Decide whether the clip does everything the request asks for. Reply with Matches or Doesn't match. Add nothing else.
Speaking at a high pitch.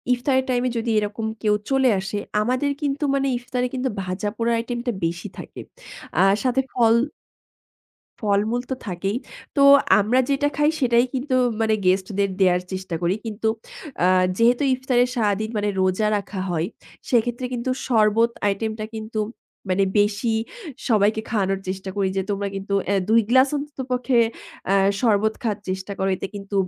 Matches